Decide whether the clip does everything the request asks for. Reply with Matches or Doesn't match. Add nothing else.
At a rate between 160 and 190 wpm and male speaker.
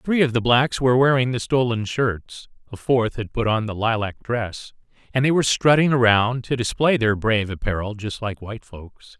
Doesn't match